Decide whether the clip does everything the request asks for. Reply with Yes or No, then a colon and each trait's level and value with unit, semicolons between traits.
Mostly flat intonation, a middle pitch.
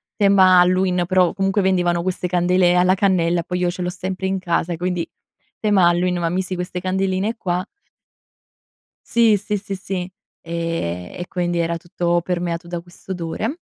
Yes: narrow, 1.5 semitones; medium, 180 Hz